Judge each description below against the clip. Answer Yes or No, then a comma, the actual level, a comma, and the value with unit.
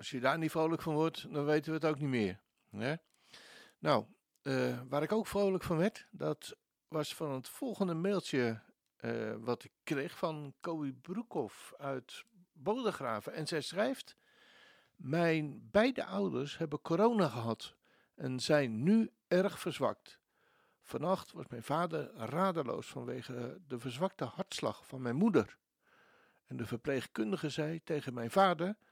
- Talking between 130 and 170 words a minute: Yes, average, 145 wpm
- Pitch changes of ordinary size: No, wide, 6.2 semitones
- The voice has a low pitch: No, medium, 155 Hz